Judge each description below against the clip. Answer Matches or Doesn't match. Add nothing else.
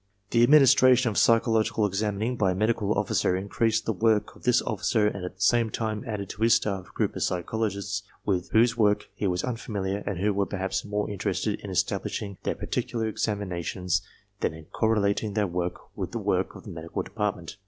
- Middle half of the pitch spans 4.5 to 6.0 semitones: Doesn't match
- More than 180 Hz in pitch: Doesn't match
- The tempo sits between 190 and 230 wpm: Matches